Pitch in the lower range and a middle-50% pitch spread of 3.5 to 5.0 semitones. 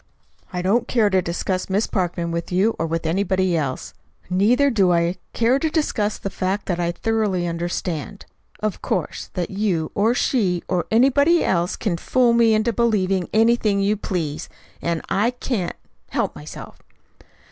No: high, 195 Hz; average, 4.5 semitones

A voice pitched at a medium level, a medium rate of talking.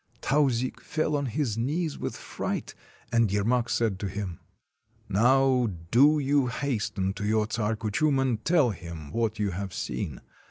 No: low, 115 Hz; average, 160 wpm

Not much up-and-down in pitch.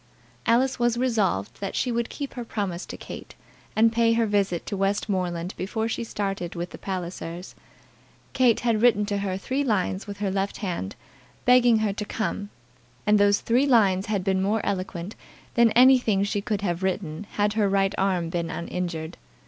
No: average, 3.5 semitones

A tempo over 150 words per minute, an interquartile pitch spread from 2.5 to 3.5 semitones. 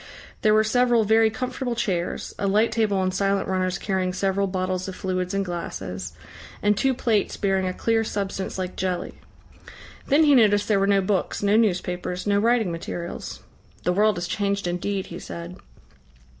Yes: average, 170 wpm; average, 2.9 semitones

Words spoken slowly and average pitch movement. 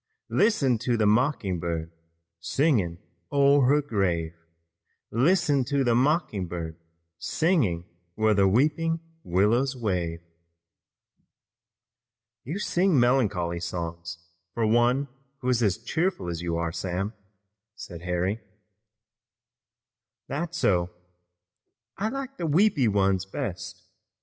No: slow, 110 wpm; wide, 8.2 semitones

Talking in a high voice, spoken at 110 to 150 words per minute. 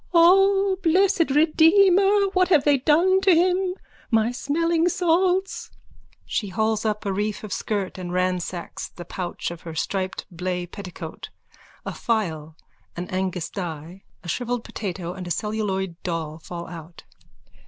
Yes: high, 215 Hz; average, 145 wpm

